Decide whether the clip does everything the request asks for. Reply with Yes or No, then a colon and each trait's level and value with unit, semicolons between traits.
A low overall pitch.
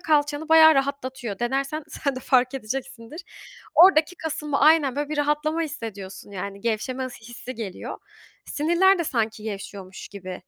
No: very high, 270 Hz